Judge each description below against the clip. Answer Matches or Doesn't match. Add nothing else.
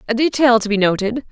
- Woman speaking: Matches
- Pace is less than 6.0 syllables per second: Doesn't match